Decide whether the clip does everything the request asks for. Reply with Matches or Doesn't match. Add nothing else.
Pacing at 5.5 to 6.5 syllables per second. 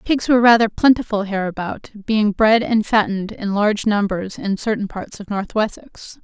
Doesn't match